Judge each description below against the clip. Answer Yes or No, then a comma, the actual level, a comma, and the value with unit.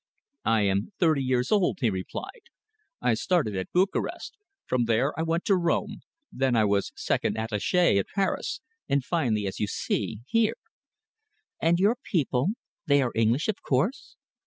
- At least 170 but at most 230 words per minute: No, average, 160 wpm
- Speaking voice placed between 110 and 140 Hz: Yes, low, 135 Hz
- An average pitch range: No, wide, 8.1 semitones